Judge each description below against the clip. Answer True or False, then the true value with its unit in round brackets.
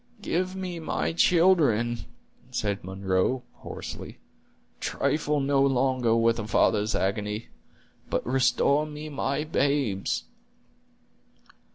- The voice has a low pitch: True (130 Hz)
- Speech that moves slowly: True (95 wpm)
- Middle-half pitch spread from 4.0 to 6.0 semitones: True (5.4 semitones)